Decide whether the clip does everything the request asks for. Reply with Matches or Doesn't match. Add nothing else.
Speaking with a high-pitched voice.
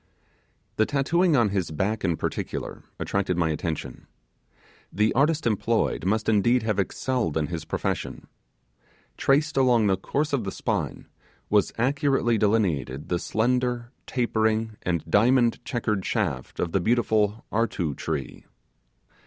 Doesn't match